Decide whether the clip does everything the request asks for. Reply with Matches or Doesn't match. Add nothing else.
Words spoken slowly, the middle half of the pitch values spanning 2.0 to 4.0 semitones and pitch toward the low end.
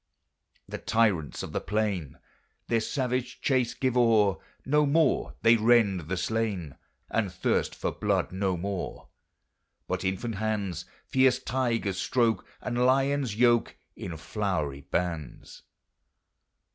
Doesn't match